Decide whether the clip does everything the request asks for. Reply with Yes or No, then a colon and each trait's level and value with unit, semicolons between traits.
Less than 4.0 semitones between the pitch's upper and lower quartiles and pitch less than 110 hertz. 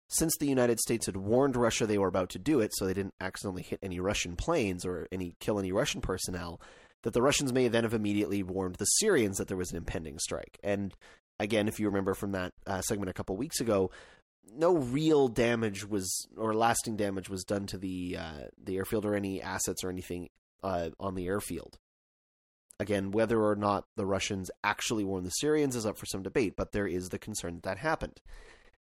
Yes: average, 2.9 semitones; low, 100 Hz